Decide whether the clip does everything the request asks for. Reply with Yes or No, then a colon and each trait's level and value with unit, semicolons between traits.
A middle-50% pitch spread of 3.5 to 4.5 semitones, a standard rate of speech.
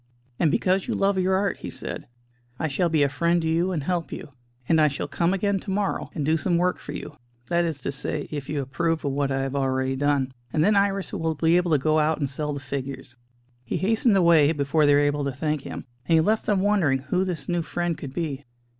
No: average, 3.9 semitones; fast, 250 wpm